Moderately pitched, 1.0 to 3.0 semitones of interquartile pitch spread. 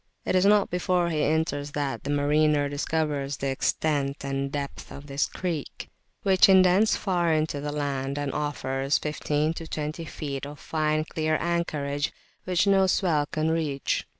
Yes: medium, 150 Hz; narrow, 2.6 semitones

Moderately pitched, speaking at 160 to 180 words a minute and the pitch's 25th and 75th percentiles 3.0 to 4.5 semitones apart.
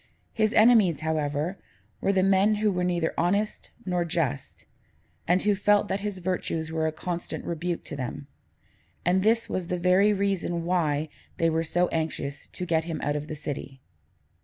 Yes: medium, 175 Hz; average, 175 wpm; average, 3.4 semitones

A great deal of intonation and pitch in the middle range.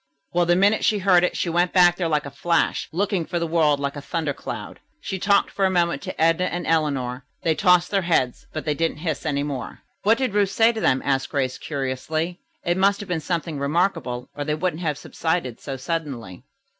No: average, 4.0 semitones; medium, 165 Hz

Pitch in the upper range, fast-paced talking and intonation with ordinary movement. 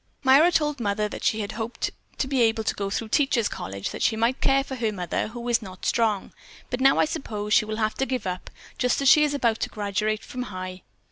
Yes: high, 225 Hz; fast, 245 wpm; average, 4.0 semitones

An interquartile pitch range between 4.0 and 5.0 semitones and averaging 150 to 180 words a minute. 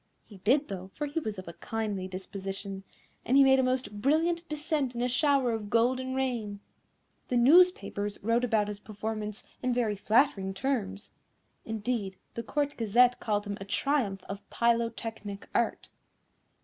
Yes: average, 4.4 semitones; average, 160 wpm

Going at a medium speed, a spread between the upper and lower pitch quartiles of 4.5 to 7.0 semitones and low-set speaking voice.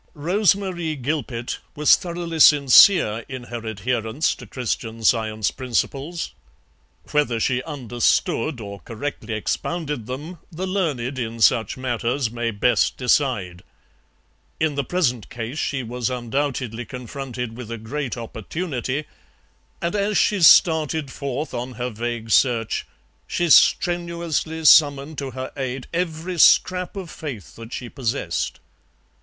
No: slow, 125 wpm; average, 5.1 semitones; low, 130 Hz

